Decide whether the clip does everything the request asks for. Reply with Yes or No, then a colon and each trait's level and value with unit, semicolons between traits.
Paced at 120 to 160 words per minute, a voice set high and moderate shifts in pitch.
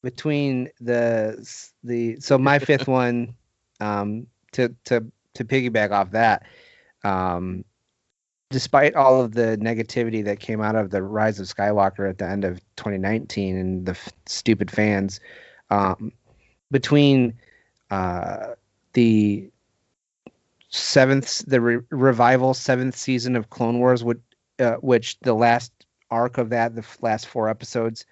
No: average, 140 wpm; low, 115 Hz; average, 3.3 semitones